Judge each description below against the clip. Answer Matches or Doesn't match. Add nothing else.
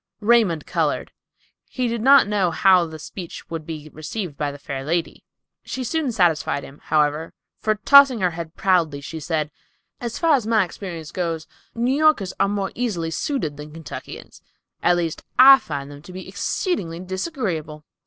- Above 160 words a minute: Matches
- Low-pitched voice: Doesn't match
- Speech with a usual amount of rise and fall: Doesn't match